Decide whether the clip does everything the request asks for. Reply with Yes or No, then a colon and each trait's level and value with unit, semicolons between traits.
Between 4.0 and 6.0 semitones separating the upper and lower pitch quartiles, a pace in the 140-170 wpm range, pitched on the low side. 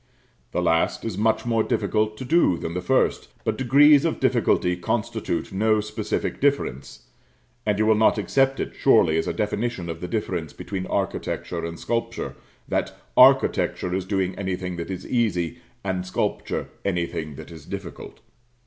Yes: average, 4.3 semitones; average, 160 wpm; low, 100 Hz